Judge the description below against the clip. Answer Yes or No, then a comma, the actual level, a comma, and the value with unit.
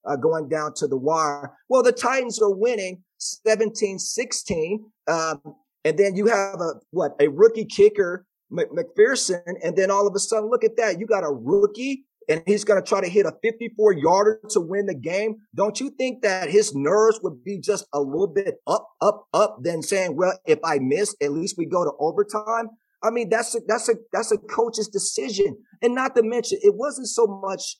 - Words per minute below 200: No, fast, 205 wpm